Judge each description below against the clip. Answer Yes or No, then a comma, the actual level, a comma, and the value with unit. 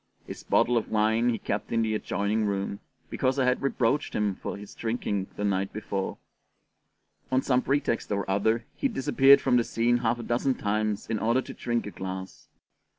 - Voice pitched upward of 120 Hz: No, low, 110 Hz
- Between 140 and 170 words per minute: No, average, 190 wpm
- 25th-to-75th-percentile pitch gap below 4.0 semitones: Yes, average, 3.2 semitones